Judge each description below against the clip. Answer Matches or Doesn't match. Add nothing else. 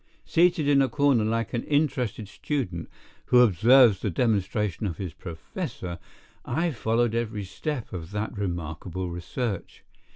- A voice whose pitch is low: Matches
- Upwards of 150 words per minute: Doesn't match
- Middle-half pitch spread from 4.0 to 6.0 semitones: Matches